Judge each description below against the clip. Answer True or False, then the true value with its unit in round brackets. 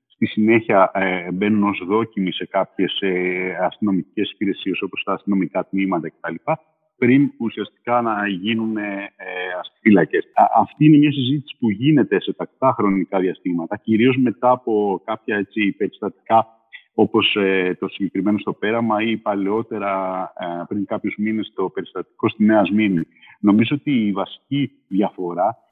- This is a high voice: False (105 Hz)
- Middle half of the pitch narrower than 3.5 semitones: True (3.1 semitones)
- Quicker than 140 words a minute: False (130 wpm)